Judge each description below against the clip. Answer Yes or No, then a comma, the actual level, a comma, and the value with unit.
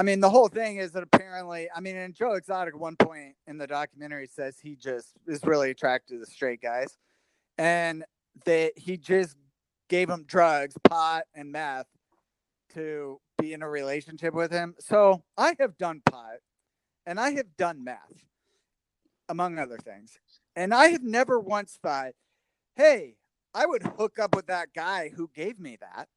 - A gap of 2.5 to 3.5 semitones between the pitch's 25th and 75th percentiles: No, average, 4.2 semitones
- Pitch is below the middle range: No, medium, 170 Hz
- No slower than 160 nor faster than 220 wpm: Yes, average, 175 wpm